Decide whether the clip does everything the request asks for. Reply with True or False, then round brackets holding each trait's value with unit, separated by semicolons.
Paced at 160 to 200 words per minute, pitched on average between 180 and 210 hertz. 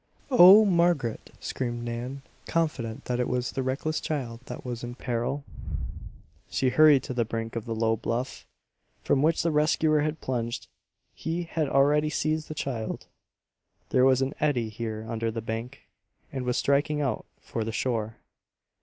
False (165 wpm; 130 Hz)